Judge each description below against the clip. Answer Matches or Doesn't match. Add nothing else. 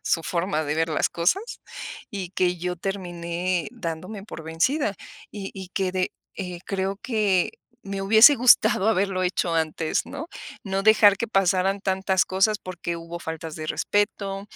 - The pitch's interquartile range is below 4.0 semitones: Matches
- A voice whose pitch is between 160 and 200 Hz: Matches